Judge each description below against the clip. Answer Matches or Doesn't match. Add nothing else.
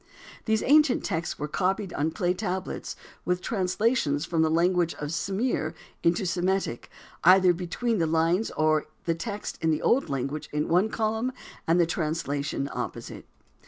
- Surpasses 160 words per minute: Doesn't match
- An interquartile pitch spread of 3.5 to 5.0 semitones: Matches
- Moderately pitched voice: Matches